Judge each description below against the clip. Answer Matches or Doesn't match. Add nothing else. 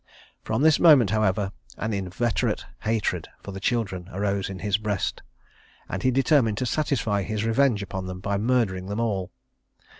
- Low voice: Matches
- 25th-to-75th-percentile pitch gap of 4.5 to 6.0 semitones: Doesn't match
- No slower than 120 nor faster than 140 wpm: Doesn't match